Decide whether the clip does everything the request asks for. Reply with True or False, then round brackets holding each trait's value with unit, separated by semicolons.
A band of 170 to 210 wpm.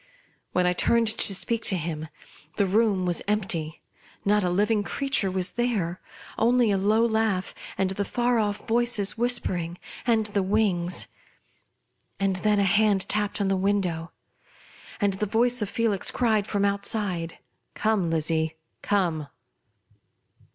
False (145 wpm)